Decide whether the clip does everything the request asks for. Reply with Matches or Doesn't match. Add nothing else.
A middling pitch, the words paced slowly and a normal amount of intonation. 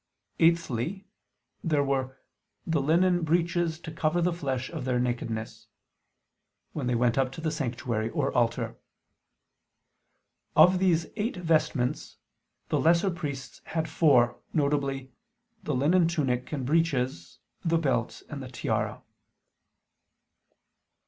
Matches